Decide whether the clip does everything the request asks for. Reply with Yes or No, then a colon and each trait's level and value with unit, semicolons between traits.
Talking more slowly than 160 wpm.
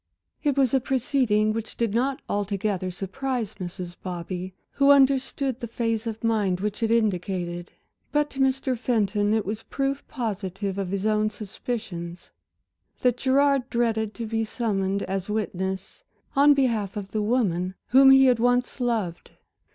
Yes: average, 150 wpm